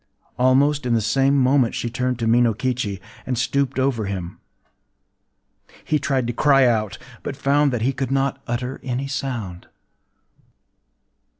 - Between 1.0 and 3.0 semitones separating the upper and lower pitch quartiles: Yes, average, 2.7 semitones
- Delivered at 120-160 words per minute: Yes, average, 140 wpm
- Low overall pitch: Yes, low, 125 Hz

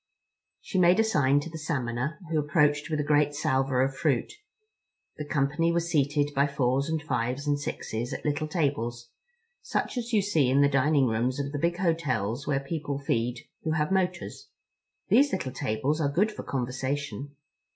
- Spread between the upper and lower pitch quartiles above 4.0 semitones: No, average, 3.2 semitones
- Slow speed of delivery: No, average, 180 wpm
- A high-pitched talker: No, medium, 145 Hz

